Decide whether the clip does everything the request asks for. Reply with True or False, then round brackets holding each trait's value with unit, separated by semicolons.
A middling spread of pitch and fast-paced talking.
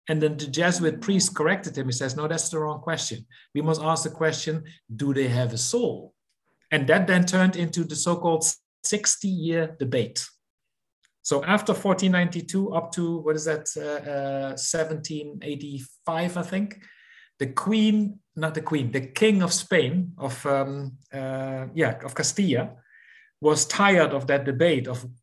False (4.3 semitones; 155 wpm)